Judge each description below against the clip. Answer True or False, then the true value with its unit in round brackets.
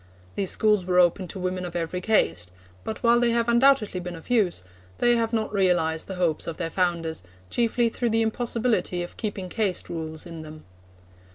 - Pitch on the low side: False (185 Hz)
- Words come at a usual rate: True (190 wpm)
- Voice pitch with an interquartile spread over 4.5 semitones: True (4.9 semitones)